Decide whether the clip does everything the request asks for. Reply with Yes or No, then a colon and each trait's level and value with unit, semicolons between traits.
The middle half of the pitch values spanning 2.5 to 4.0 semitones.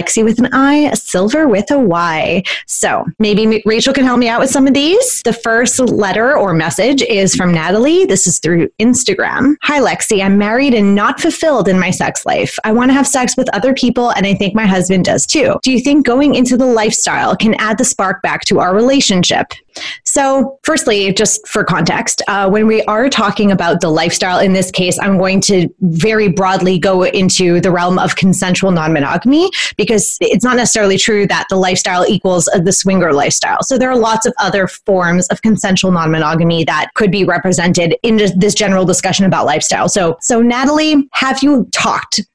No: average, 4.8 semitones